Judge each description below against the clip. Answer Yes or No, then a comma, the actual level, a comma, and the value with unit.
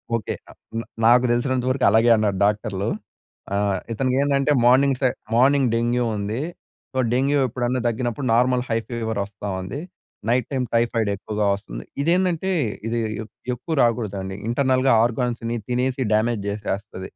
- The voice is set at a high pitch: No, low, 120 Hz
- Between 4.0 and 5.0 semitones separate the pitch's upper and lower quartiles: No, average, 3.3 semitones